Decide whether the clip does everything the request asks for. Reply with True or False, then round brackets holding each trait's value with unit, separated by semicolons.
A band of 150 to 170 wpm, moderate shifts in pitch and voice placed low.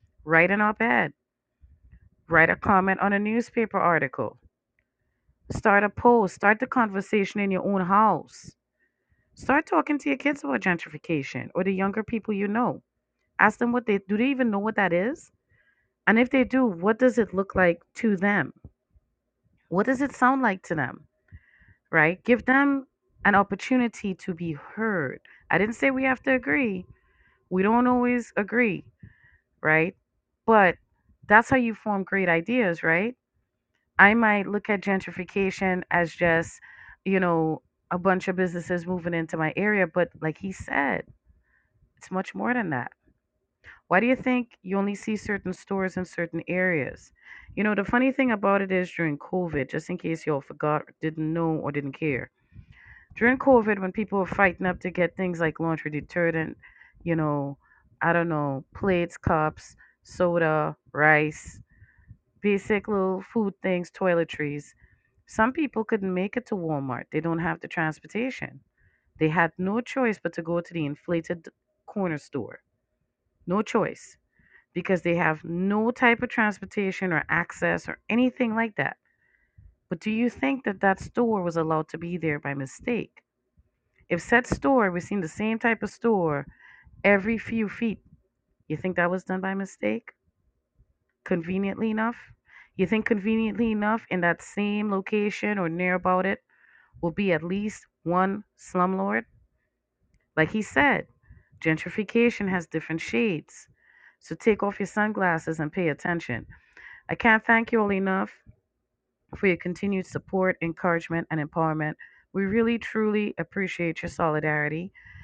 False (155 wpm; 4.7 semitones; 190 Hz)